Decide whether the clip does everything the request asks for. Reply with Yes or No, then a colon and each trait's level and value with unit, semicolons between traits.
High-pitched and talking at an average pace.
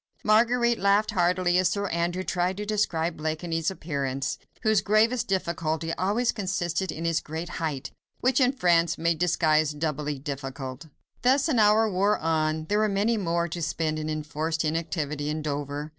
No: medium, 170 Hz; average, 160 wpm